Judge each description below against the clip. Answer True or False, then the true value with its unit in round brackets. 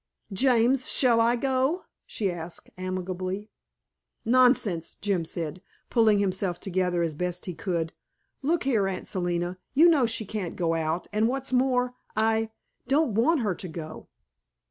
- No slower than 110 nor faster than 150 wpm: True (145 wpm)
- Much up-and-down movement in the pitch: True (5.8 semitones)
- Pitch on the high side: True (205 Hz)